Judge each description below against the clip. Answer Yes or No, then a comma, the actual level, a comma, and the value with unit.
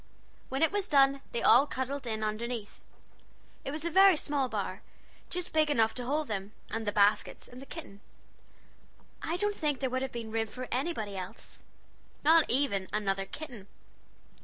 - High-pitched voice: Yes, very high, 255 Hz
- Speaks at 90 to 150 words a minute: No, average, 175 wpm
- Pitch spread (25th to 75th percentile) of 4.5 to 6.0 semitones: Yes, wide, 5.6 semitones